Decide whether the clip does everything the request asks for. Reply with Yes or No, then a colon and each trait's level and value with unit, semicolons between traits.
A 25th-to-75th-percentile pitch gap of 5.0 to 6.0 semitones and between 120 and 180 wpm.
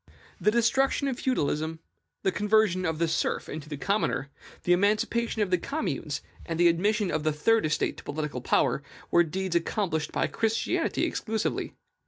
Yes: wide, 5.5 semitones; average, 165 wpm